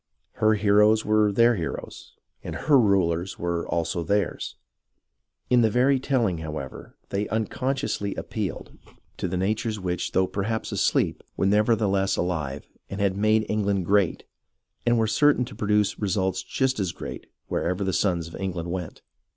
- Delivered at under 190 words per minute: Yes, average, 155 wpm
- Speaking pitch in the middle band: No, low, 100 Hz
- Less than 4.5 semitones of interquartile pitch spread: Yes, average, 3.1 semitones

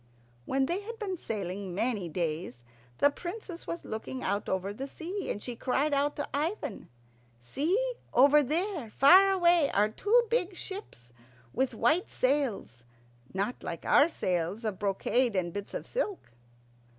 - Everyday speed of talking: Yes, average, 150 wpm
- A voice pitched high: Yes, very high, 270 Hz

